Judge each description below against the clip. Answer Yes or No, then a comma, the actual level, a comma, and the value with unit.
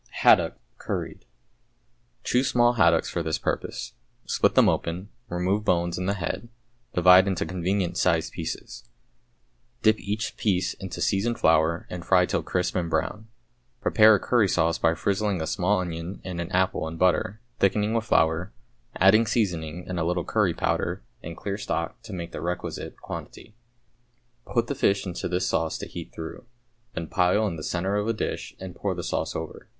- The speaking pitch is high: No, very low, 90 Hz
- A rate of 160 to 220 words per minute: Yes, average, 175 wpm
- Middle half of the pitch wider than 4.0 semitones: No, average, 3.3 semitones